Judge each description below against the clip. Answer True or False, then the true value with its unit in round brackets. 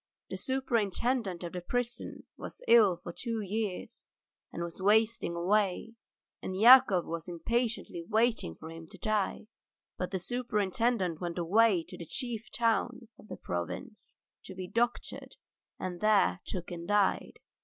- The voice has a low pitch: False (205 Hz)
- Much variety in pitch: False (4.7 semitones)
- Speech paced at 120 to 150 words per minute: True (145 wpm)